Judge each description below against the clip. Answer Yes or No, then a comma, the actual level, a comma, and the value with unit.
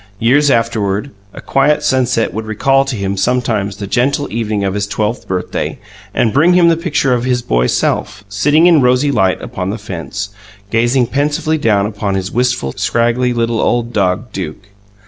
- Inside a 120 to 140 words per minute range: No, average, 175 wpm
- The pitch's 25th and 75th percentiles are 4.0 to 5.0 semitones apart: Yes, average, 4.7 semitones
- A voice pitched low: Yes, low, 115 Hz